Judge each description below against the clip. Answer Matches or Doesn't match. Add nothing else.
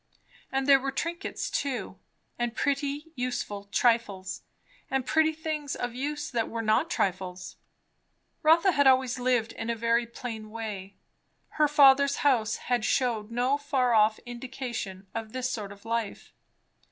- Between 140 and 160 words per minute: Matches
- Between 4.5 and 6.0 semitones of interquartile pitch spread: Doesn't match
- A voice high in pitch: Matches